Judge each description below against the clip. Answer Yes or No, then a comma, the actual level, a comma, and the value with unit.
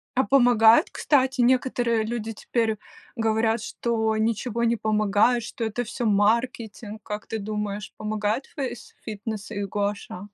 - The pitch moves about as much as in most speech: No, narrow, 2.2 semitones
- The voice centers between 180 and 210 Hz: No, high, 220 Hz